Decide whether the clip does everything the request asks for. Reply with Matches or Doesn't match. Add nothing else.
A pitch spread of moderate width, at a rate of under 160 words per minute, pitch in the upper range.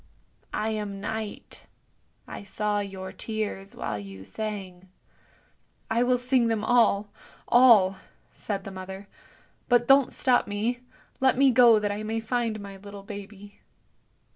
Matches